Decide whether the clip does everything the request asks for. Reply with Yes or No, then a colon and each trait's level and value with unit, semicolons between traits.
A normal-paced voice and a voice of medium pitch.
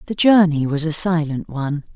Yes: average, 185 wpm; medium, 160 Hz